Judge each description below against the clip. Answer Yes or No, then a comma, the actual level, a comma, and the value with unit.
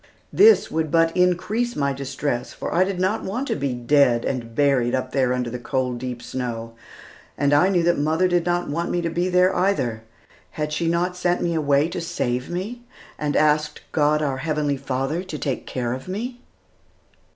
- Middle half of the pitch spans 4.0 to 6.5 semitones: Yes, average, 5.2 semitones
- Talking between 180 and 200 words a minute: Yes, average, 195 wpm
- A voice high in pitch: No, medium, 150 Hz